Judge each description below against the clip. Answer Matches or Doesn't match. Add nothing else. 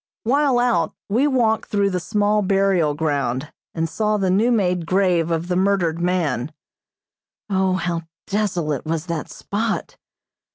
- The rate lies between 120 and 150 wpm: Matches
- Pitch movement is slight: Doesn't match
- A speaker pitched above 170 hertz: Matches